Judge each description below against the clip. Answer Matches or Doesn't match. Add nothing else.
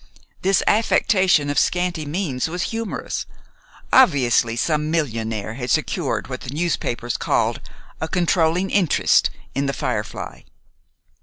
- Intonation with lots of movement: Matches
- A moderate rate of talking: Doesn't match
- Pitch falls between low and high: Matches